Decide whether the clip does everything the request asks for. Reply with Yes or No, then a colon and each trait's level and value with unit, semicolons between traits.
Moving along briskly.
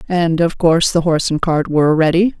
Yes: fast, 225 wpm